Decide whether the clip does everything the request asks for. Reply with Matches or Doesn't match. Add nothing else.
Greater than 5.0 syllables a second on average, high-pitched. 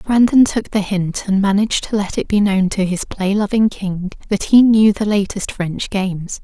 Doesn't match